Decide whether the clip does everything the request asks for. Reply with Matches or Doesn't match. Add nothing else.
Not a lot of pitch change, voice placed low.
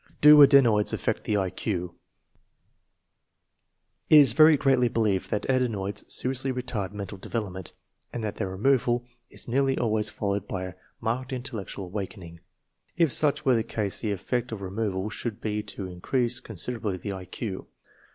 Doesn't match